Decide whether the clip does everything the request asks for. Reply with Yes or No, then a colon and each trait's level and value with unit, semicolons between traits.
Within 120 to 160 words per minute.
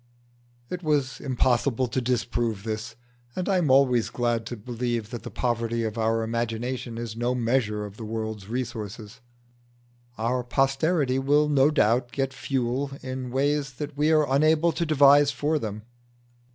Yes: average, 155 wpm